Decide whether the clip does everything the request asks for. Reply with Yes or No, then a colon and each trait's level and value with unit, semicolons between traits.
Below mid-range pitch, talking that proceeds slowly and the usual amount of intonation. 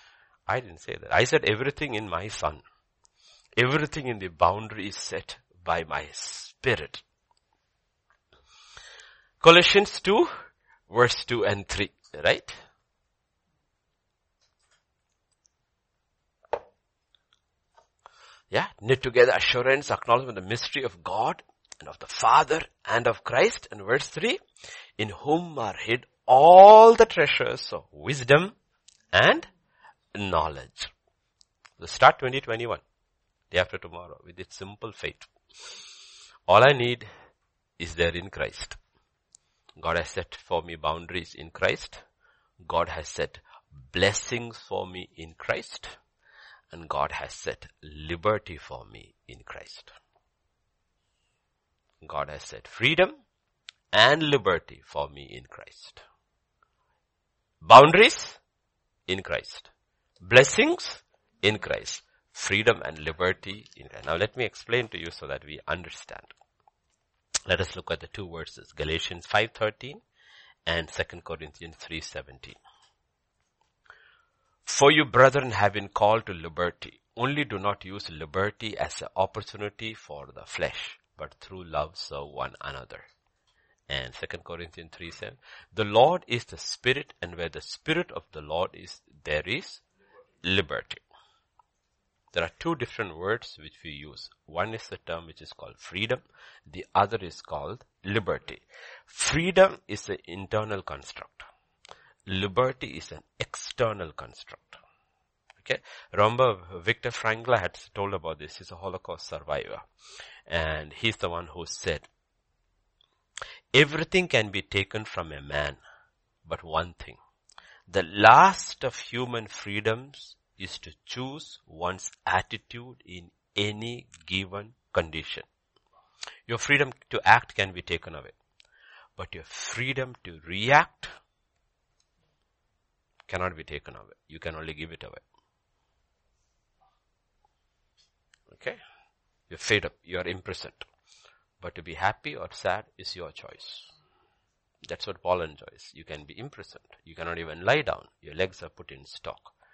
No: low, 100 Hz; slow, 130 wpm; wide, 6.9 semitones